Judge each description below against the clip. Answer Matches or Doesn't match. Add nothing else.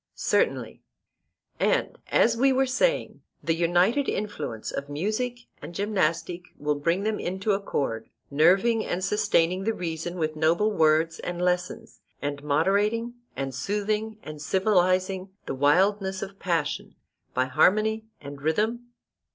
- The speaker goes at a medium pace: Doesn't match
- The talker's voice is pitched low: Doesn't match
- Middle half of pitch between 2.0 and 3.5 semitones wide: Doesn't match